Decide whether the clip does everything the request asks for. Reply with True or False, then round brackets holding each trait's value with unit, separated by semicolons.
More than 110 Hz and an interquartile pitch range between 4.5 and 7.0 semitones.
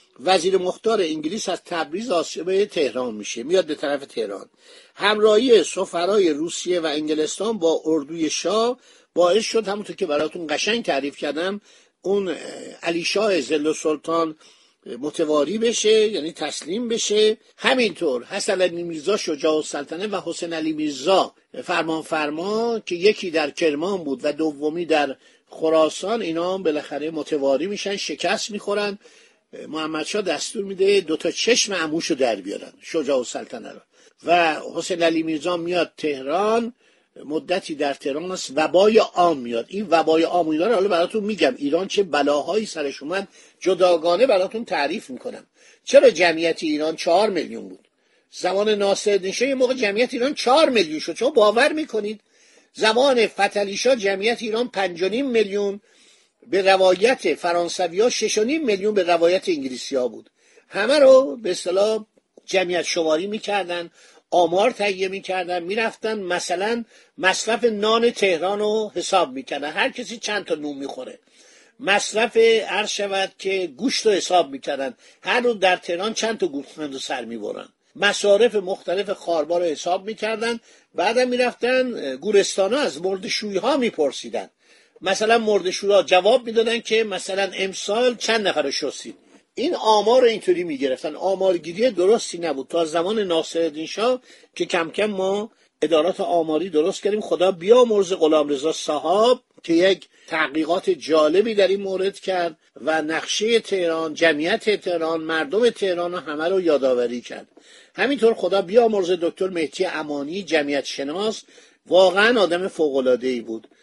True (190 Hz; 5.1 semitones)